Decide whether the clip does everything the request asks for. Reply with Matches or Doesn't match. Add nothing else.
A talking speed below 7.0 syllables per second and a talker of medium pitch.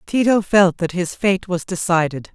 Matches